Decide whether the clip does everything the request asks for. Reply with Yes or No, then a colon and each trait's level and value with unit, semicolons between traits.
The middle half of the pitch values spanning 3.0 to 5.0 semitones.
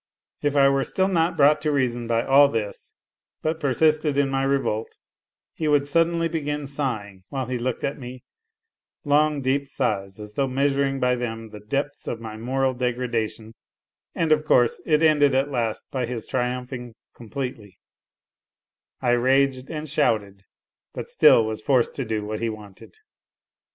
Yes: average, 3.8 semitones